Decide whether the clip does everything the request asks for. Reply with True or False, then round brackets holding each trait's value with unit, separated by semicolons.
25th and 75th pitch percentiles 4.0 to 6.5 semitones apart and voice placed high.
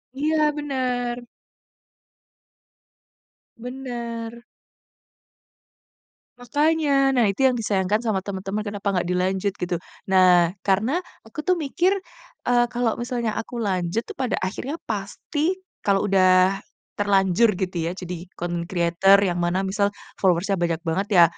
True (4.9 semitones; 205 Hz)